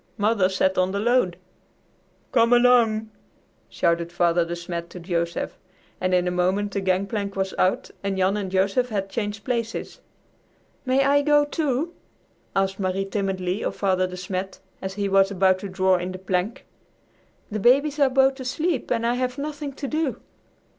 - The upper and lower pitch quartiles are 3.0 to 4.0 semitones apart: No, average, 5.0 semitones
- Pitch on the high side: Yes, high, 200 Hz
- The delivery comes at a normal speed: Yes, average, 170 wpm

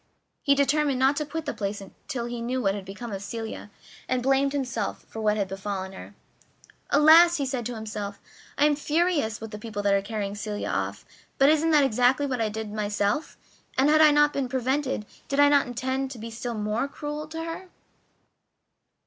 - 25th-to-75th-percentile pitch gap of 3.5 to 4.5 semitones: No, average, 5.3 semitones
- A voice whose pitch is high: Yes, very high, 250 Hz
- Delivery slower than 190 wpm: No, fast, 205 wpm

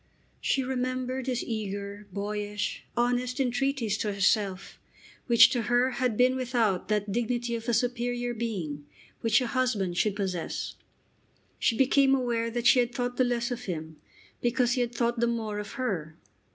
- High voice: Yes, high, 235 Hz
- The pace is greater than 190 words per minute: No, average, 165 wpm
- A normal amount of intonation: Yes, average, 3.1 semitones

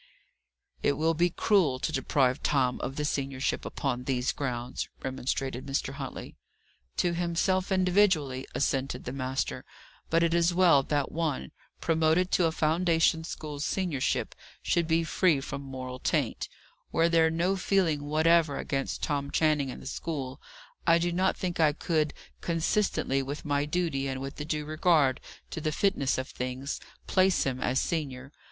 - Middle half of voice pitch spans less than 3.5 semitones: No, average, 3.8 semitones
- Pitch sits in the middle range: Yes, medium, 150 Hz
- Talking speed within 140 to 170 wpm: Yes, average, 160 wpm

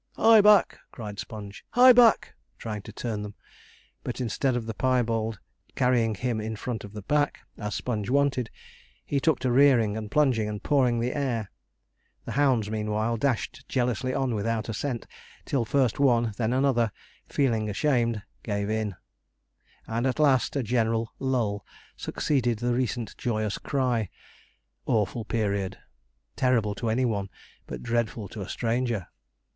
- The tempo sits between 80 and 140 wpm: No, average, 155 wpm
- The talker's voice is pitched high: No, low, 115 Hz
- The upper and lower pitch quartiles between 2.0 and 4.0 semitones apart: Yes, average, 3.1 semitones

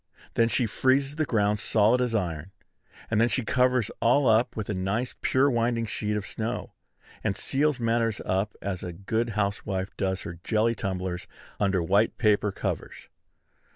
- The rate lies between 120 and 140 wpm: No, average, 165 wpm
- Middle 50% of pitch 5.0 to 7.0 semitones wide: No, average, 3.3 semitones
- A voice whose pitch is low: Yes, low, 110 Hz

